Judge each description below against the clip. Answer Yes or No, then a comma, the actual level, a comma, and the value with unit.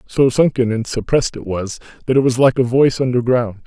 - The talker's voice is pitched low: Yes, low, 125 Hz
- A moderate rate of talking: No, fast, 215 wpm